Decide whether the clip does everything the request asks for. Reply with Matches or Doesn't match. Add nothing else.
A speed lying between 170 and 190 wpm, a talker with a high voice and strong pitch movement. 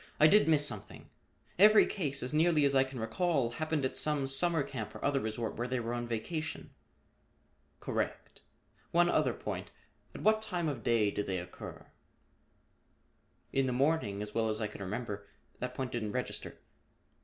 Doesn't match